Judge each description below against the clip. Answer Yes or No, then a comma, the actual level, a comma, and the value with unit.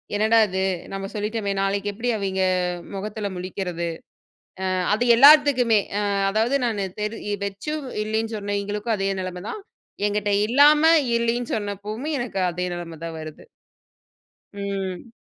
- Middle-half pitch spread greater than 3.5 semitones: No, average, 2.8 semitones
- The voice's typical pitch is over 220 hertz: No, high, 205 Hz